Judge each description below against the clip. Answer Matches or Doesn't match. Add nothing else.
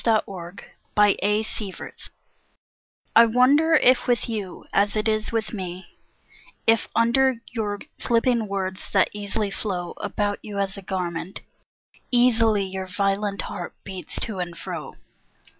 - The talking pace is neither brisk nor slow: Doesn't match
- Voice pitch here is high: Matches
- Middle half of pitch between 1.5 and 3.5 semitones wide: Matches